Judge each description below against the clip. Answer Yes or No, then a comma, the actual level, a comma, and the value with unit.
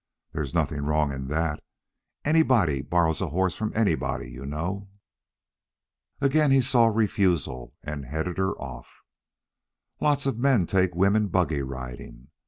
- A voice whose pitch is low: Yes, very low, 85 Hz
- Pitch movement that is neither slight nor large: No, wide, 7.1 semitones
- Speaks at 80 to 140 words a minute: Yes, slow, 135 wpm